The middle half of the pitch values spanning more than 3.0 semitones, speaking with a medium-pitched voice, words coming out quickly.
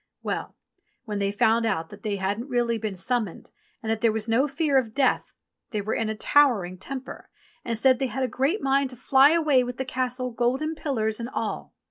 No: average, 3.6 semitones; high, 245 Hz; fast, 210 wpm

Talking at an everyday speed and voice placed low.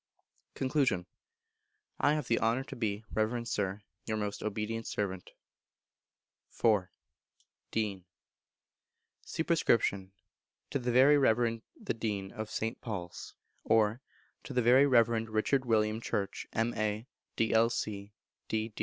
No: slow, 115 wpm; low, 110 Hz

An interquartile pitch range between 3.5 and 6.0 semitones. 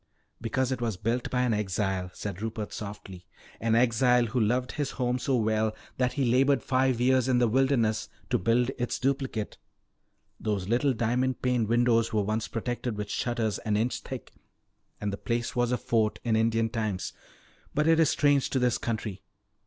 No: narrow, 2.6 semitones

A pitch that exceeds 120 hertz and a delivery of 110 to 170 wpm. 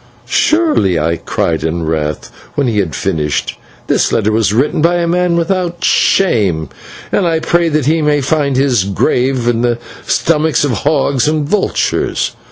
Yes: medium, 140 Hz; average, 165 wpm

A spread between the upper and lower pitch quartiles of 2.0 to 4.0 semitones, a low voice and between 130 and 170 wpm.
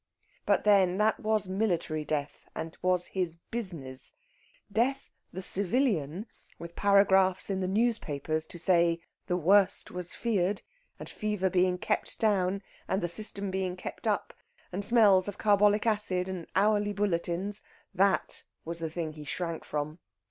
No: average, 3.2 semitones; medium, 185 Hz; average, 150 wpm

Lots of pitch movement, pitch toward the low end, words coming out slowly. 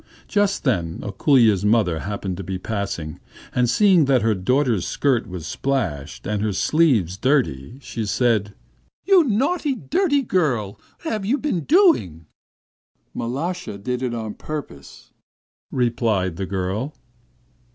Yes: wide, 8.3 semitones; low, 115 Hz; slow, 130 wpm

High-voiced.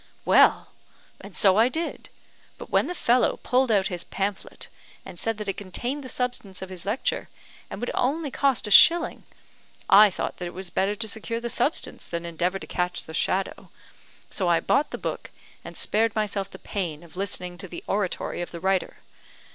Yes: high, 200 Hz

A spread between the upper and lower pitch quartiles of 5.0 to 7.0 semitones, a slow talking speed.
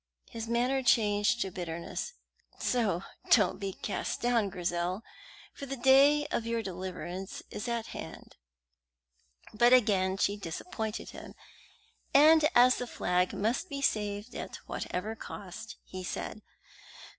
No: average, 4.6 semitones; slow, 130 wpm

